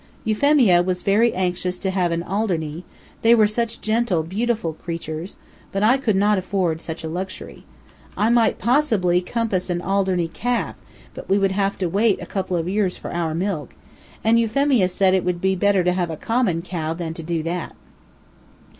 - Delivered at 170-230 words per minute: Yes, average, 185 wpm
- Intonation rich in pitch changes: No, average, 3.7 semitones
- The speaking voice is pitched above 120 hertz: Yes, high, 190 Hz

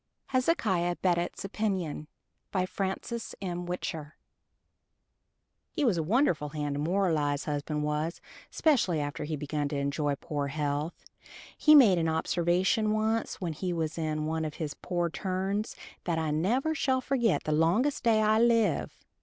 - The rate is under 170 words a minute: Yes, average, 150 wpm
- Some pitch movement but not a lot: No, wide, 5.8 semitones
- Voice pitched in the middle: Yes, medium, 175 Hz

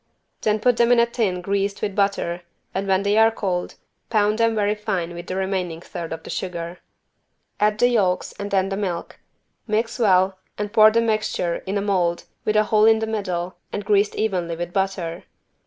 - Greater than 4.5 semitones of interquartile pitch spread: No, average, 2.9 semitones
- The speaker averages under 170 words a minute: No, average, 195 wpm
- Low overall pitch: No, high, 200 Hz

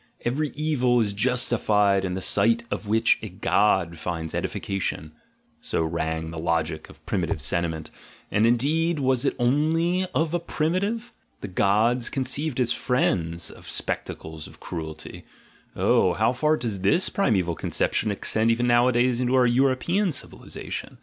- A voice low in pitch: Yes, low, 115 Hz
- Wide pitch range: Yes, wide, 6.4 semitones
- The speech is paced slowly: No, average, 150 wpm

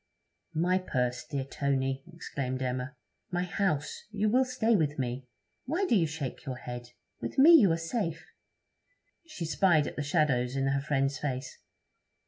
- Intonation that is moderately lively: No, wide, 5.7 semitones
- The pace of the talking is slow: No, average, 160 wpm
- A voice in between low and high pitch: Yes, medium, 145 Hz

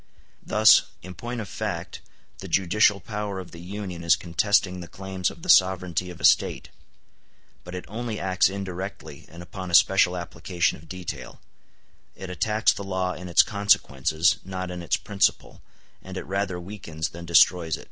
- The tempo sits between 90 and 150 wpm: No, average, 175 wpm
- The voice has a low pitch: Yes, very low, 90 Hz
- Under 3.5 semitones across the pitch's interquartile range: Yes, narrow, 2.4 semitones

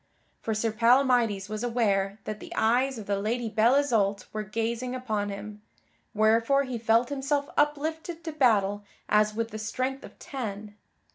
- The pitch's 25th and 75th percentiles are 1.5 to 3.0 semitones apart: No, average, 3.4 semitones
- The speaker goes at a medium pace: Yes, average, 160 wpm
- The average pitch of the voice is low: No, high, 230 Hz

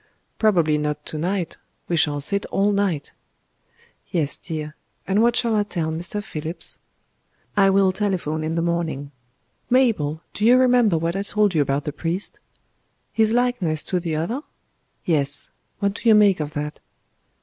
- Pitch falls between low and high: Yes, medium, 175 Hz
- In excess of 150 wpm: Yes, average, 160 wpm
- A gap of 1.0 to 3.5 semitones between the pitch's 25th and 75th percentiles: No, average, 5.0 semitones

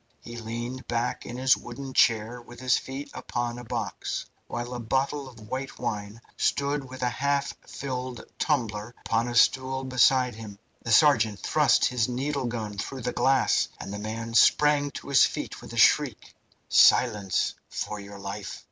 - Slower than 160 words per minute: No, average, 170 wpm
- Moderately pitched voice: No, low, 120 Hz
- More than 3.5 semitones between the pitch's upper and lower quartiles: No, average, 2.9 semitones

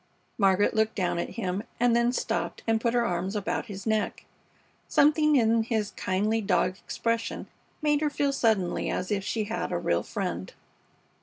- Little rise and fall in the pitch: No, average, 3.2 semitones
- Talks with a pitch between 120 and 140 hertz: No, high, 220 Hz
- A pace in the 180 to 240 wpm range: No, average, 170 wpm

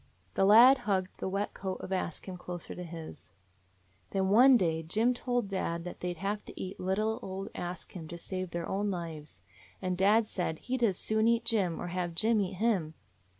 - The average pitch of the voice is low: No, high, 190 Hz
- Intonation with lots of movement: No, average, 3.5 semitones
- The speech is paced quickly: Yes, fast, 210 wpm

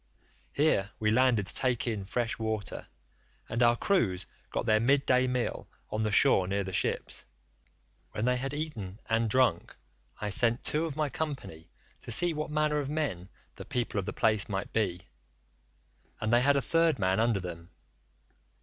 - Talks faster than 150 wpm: Yes, average, 175 wpm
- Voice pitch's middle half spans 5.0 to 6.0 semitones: Yes, wide, 5.6 semitones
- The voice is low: Yes, low, 115 Hz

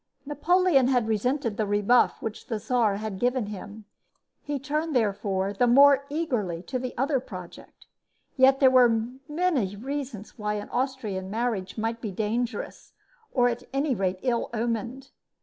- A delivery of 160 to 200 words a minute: No, average, 150 wpm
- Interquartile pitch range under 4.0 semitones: No, average, 4.3 semitones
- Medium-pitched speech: No, high, 240 Hz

